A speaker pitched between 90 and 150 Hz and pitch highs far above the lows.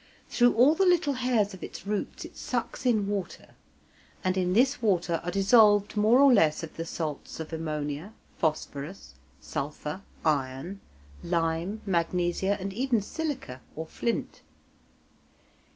No: high, 190 Hz; wide, 6.0 semitones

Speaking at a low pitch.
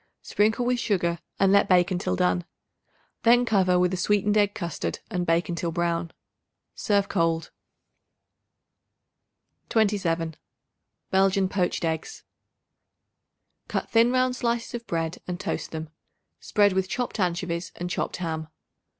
No: medium, 185 Hz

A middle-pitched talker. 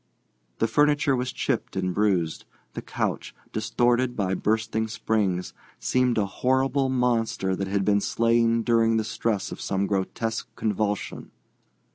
No: low, 110 Hz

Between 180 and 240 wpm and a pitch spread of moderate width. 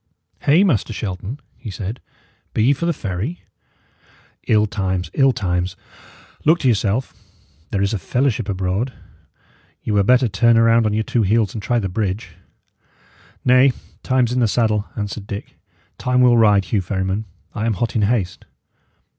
No: average, 165 wpm; average, 3.9 semitones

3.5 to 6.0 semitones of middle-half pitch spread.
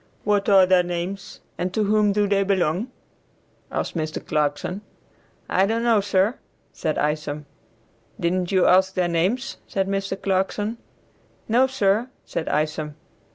No: average, 3.1 semitones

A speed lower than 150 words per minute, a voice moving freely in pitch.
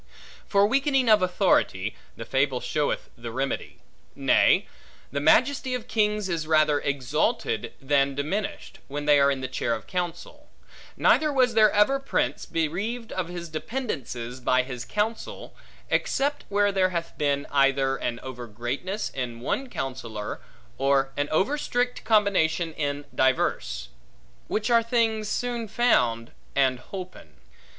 Yes: average, 140 wpm; wide, 8.2 semitones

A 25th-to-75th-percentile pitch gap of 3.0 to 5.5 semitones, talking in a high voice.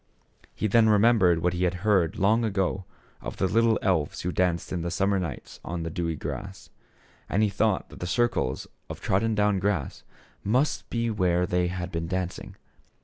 No: average, 3.5 semitones; very low, 95 Hz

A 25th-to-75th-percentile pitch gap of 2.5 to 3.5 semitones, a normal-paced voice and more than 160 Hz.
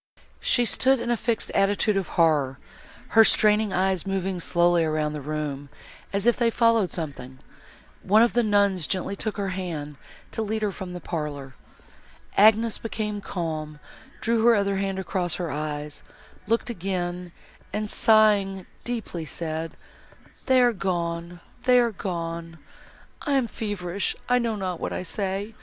No: average, 4.6 semitones; average, 150 wpm; high, 190 Hz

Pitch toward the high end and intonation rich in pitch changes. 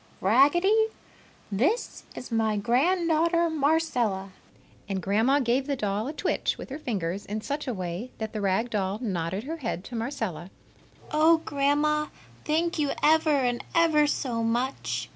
Yes: very high, 255 Hz; wide, 6.3 semitones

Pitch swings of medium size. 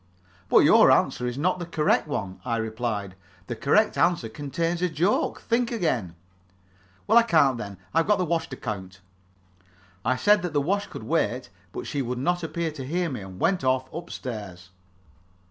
No: wide, 7.2 semitones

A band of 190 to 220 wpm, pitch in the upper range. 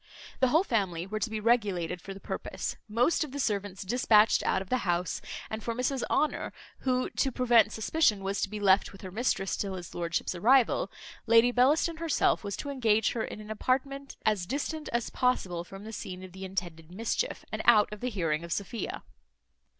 Yes: average, 200 wpm; high, 215 Hz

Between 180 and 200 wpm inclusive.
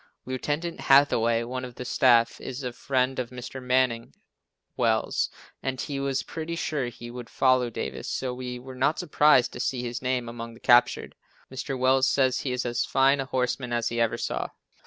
Yes: average, 190 wpm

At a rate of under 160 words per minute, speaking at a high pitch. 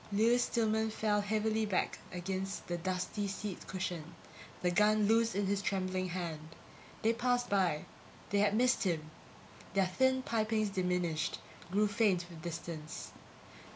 Yes: average, 145 wpm; high, 200 Hz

